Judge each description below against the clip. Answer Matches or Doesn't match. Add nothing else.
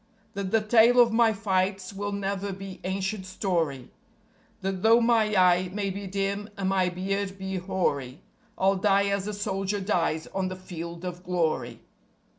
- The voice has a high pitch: Matches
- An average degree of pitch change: Doesn't match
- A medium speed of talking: Matches